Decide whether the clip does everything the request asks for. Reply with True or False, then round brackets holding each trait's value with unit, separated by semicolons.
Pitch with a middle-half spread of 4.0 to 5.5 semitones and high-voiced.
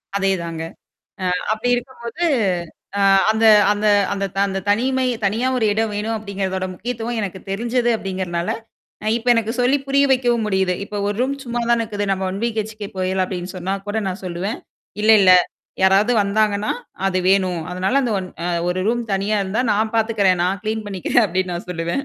False (3.2 semitones; 205 Hz)